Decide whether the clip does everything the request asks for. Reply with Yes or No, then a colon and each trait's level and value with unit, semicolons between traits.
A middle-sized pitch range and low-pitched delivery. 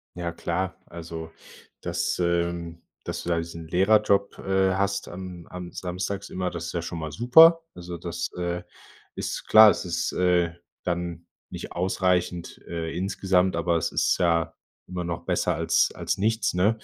No: narrow, 1.9 semitones; very low, 90 Hz